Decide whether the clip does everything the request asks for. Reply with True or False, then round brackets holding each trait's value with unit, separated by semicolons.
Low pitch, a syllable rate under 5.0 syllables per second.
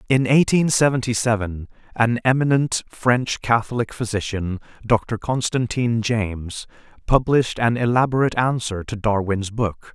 True (115 Hz; 4.5 syllables/s)